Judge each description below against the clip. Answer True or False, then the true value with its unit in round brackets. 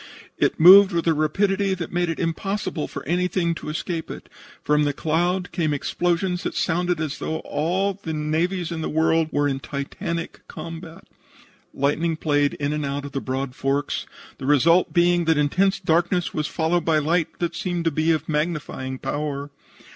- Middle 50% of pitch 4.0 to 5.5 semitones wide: False (2.8 semitones)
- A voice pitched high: False (165 Hz)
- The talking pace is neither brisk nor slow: True (175 wpm)